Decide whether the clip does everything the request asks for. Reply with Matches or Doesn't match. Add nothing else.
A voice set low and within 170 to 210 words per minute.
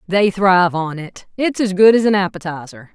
Doesn't match